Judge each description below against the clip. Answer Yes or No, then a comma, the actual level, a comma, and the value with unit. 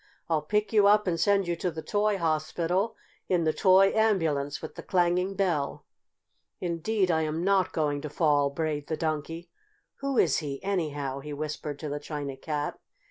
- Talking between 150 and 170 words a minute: No, average, 180 wpm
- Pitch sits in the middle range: Yes, medium, 165 Hz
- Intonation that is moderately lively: Yes, average, 4.3 semitones